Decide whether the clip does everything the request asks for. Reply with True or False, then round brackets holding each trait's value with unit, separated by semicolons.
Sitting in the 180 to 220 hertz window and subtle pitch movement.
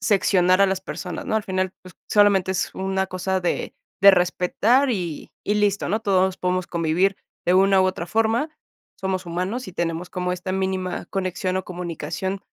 True (185 Hz; 1.5 semitones)